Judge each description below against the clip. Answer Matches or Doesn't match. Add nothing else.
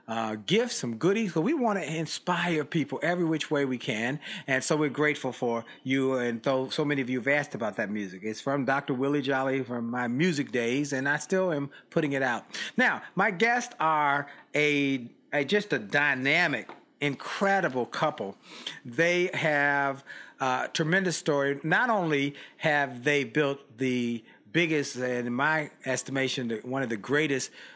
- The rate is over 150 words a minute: Matches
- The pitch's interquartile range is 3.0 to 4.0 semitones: Matches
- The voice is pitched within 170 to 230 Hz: Doesn't match